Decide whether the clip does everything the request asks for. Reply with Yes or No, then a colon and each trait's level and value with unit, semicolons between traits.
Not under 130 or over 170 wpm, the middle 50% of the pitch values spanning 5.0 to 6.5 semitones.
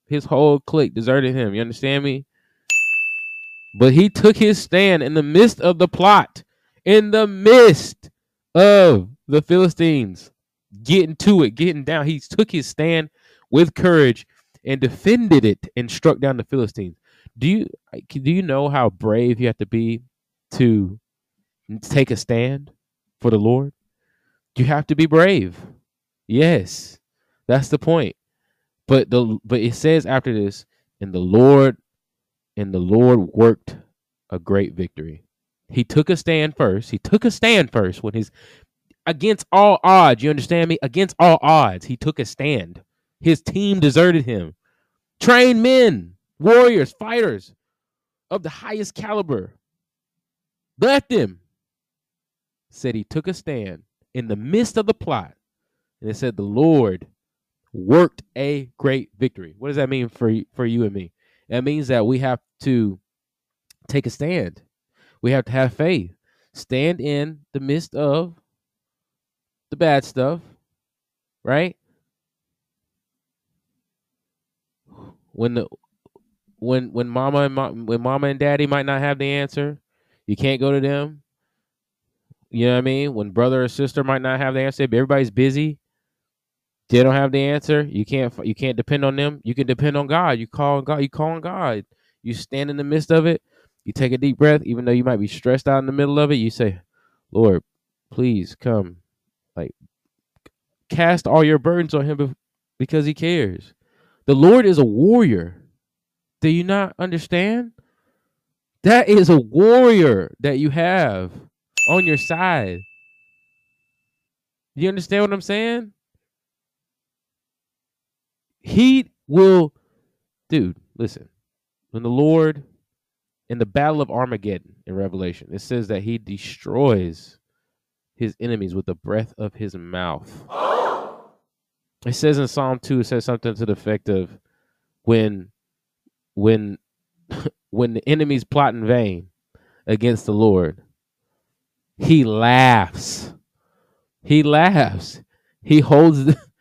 Yes: average, 150 wpm; wide, 5.6 semitones